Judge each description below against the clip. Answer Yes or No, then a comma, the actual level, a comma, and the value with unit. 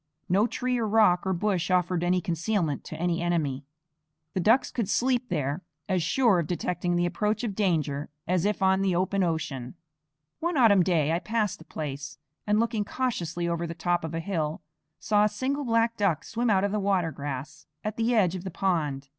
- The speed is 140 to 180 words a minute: No, average, 200 wpm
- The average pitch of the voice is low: No, medium, 185 Hz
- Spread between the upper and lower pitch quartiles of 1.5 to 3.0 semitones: No, average, 4.3 semitones